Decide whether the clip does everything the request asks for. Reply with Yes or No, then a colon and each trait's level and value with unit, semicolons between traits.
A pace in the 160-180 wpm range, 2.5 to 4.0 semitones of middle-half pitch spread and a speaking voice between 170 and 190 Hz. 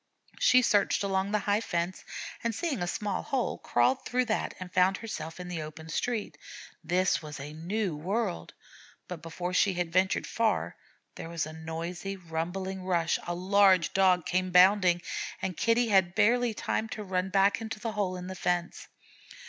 Yes: average, 175 wpm; average, 3.1 semitones; medium, 185 Hz